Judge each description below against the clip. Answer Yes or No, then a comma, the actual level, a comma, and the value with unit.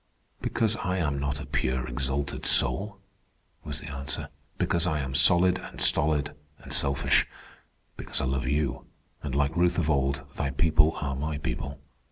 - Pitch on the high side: No, very low, 70 Hz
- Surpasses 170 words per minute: No, average, 165 wpm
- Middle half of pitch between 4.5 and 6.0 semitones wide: No, average, 2.8 semitones